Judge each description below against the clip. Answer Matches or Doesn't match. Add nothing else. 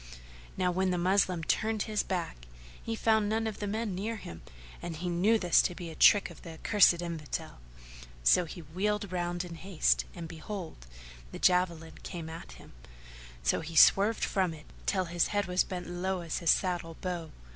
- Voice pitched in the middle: Matches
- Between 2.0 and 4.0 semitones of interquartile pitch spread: Matches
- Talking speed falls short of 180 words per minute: Doesn't match